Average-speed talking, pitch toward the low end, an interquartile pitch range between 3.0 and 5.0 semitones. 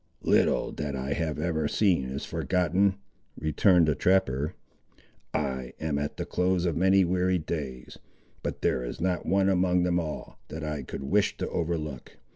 Yes: average, 165 wpm; very low, 80 Hz; average, 4.0 semitones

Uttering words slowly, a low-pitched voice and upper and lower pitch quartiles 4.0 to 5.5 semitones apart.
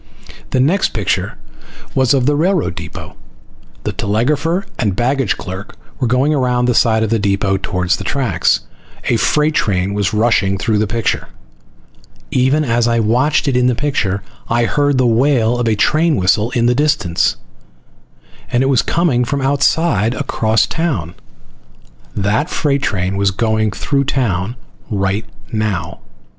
No: average, 155 wpm; low, 120 Hz; average, 5.2 semitones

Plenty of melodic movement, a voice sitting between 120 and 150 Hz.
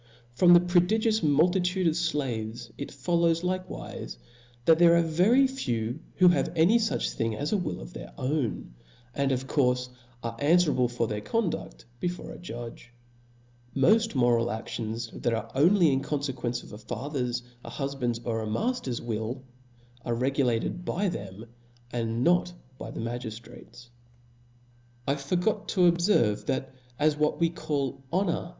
Yes: wide, 6.7 semitones; medium, 140 Hz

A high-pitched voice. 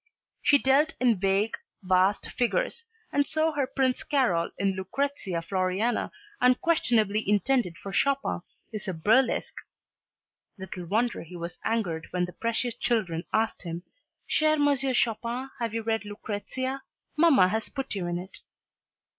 Yes: high, 225 Hz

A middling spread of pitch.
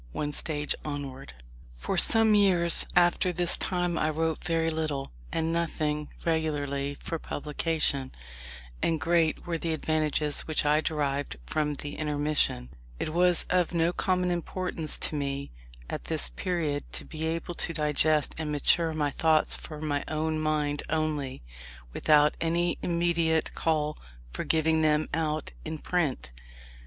No: narrow, 2.1 semitones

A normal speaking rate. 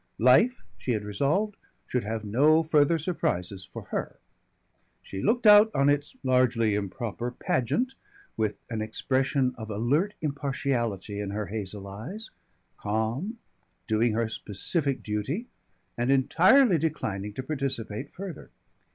No: slow, 125 wpm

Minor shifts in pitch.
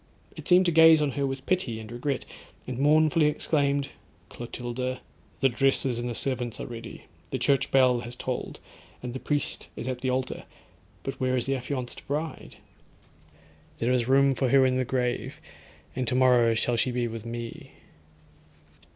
Yes: narrow, 2.2 semitones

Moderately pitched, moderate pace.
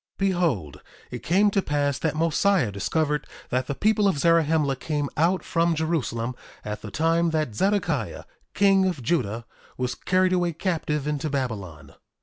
Yes: medium, 155 Hz; average, 155 wpm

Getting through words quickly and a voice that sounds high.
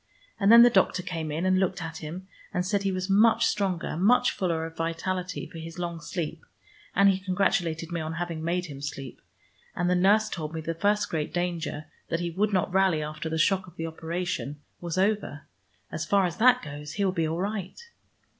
No: fast, 210 wpm; medium, 175 Hz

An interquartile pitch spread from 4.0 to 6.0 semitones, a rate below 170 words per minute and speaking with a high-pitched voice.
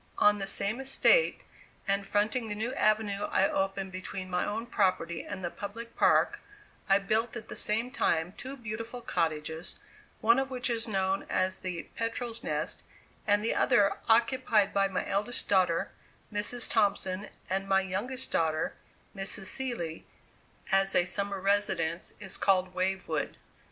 No: average, 3.3 semitones; average, 150 wpm; high, 200 Hz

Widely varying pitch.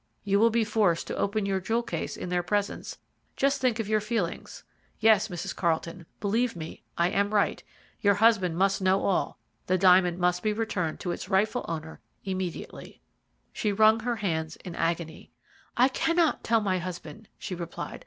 No: average, 3.7 semitones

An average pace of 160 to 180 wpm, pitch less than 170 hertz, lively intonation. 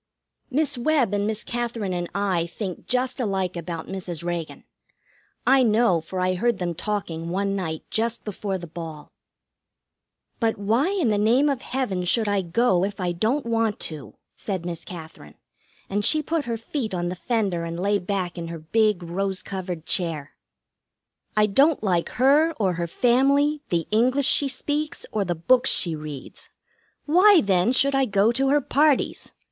No: average, 175 wpm; high, 205 Hz; wide, 6.2 semitones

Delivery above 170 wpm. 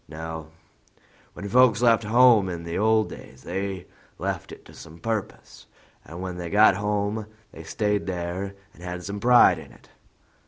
No: average, 165 wpm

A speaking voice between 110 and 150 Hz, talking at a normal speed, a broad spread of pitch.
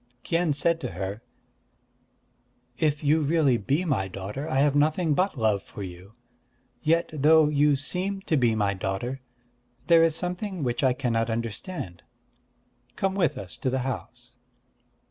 Yes: medium, 140 Hz; average, 150 wpm; wide, 6.2 semitones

